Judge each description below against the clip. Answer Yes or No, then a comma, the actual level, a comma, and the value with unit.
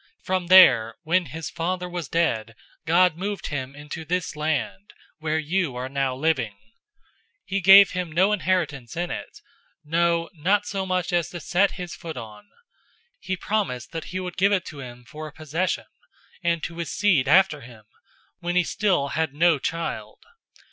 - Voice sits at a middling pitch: Yes, medium, 165 Hz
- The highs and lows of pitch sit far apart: No, average, 4.0 semitones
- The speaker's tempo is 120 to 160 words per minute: No, average, 175 wpm